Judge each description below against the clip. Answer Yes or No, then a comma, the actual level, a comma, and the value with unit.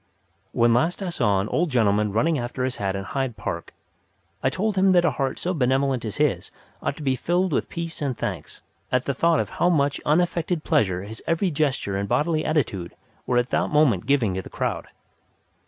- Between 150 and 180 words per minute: No, fast, 205 wpm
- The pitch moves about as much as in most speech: No, wide, 6.8 semitones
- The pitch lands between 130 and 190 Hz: Yes, low, 135 Hz